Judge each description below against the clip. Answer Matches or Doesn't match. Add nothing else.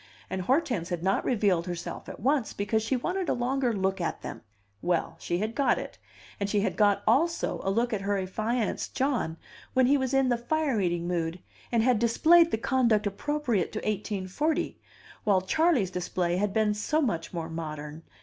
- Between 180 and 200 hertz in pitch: Doesn't match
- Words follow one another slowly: Doesn't match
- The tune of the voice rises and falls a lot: Matches